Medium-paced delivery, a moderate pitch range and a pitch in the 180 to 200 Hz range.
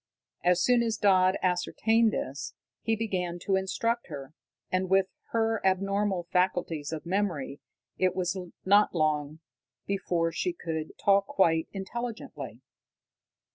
No: slow, 125 wpm; average, 3.7 semitones; medium, 185 Hz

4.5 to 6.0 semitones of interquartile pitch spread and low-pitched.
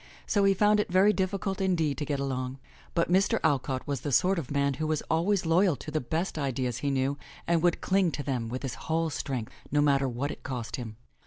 No: average, 4.9 semitones; medium, 145 Hz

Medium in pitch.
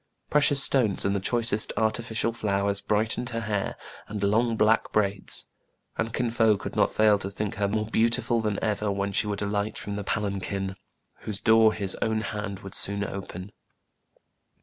No: low, 105 Hz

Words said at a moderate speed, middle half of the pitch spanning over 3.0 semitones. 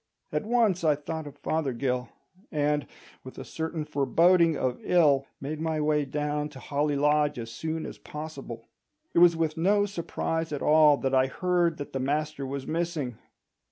No: average, 170 wpm; narrow, 2.6 semitones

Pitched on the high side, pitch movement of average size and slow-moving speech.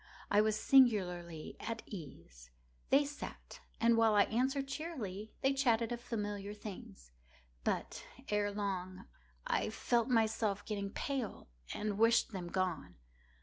Yes: high, 210 Hz; average, 3.6 semitones; slow, 130 wpm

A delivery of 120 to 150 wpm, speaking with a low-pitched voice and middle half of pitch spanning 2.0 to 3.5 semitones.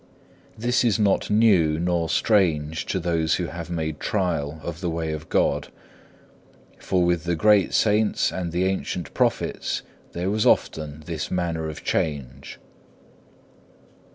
Yes: average, 140 wpm; very low, 85 Hz; average, 3.2 semitones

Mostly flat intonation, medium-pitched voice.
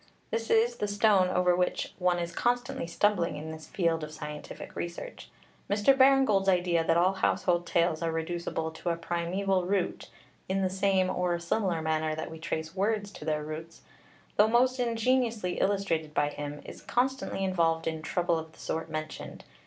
No: average, 4.0 semitones; medium, 180 Hz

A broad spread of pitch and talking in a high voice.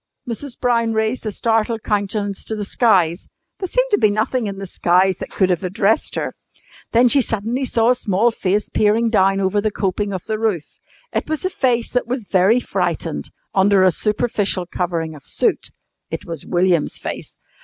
No: average, 3.7 semitones; high, 210 Hz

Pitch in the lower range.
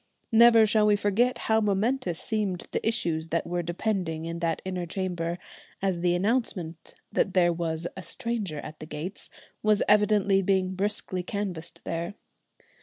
No: high, 190 Hz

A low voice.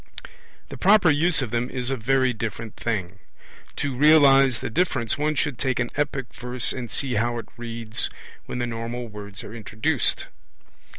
Yes: low, 125 Hz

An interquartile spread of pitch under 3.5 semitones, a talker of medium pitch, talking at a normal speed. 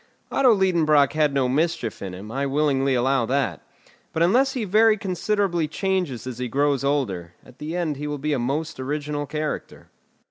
No: average, 4.4 semitones; medium, 145 Hz; average, 180 wpm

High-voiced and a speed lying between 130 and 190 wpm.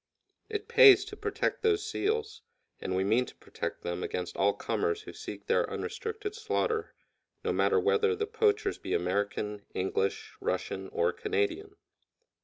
Yes: very high, 425 Hz; average, 150 wpm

